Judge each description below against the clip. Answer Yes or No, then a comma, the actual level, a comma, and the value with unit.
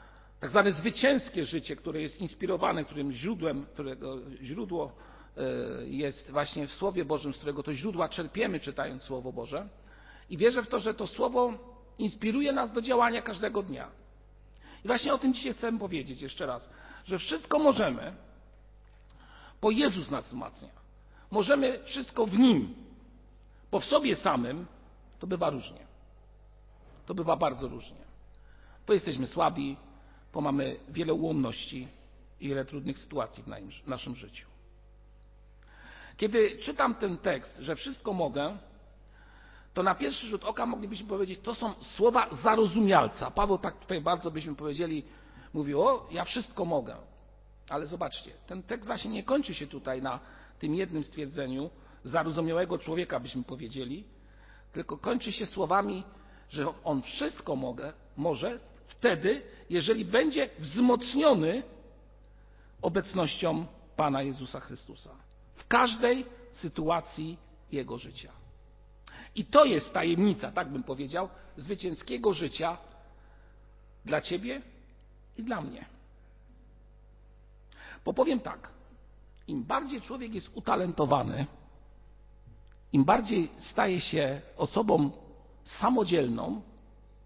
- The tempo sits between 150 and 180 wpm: No, average, 120 wpm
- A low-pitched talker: No, medium, 165 Hz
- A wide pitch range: Yes, wide, 8.3 semitones